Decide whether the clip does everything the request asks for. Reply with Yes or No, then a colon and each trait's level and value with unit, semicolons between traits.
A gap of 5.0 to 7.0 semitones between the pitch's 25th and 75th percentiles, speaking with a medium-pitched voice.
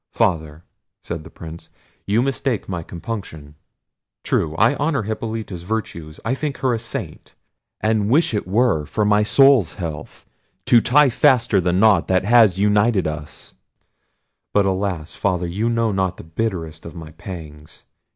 No: wide, 5.4 semitones; low, 100 Hz